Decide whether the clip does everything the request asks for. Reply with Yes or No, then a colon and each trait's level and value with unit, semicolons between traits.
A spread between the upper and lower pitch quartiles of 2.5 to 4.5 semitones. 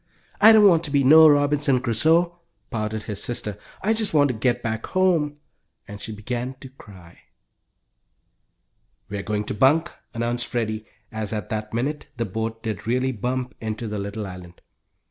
No: average, 5.0 semitones